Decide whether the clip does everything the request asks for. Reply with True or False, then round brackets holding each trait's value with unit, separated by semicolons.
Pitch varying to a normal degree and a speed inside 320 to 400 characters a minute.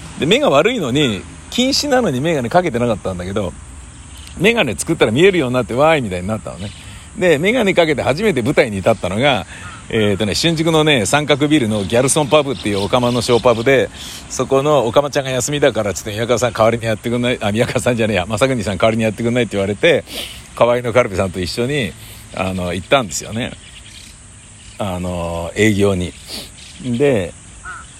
False (4.7 semitones; 435 characters per minute)